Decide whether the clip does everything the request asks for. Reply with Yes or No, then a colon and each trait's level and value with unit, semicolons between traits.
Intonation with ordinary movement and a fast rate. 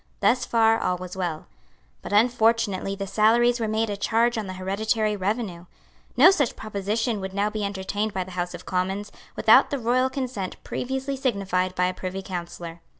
No: average, 3.6 semitones; average, 180 wpm